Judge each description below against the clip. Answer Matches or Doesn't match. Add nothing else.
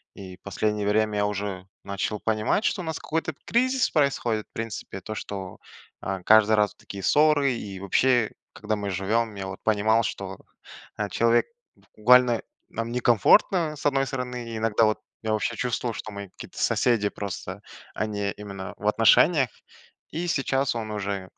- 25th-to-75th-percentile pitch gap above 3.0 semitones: Matches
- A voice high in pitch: Doesn't match